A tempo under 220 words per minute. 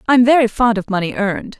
No: fast, 225 wpm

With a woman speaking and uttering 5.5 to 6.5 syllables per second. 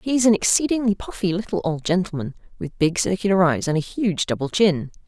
Yes: female; 5.9 syllables/s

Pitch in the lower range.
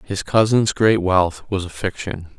Yes: very low, 95 Hz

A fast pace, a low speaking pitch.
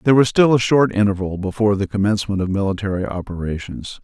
No: average, 180 wpm; low, 100 Hz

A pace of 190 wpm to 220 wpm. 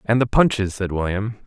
Yes: fast, 205 wpm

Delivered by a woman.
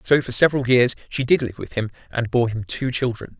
No: male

